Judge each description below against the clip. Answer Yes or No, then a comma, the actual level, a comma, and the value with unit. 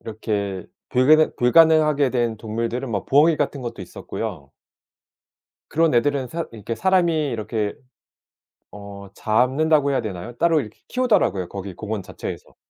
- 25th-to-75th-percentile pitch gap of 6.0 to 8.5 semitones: Yes, wide, 6.3 semitones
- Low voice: Yes, low, 125 Hz